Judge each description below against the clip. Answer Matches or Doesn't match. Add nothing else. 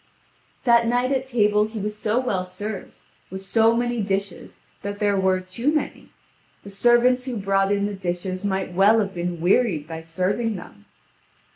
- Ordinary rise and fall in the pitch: Matches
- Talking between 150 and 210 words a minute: Matches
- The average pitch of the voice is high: Matches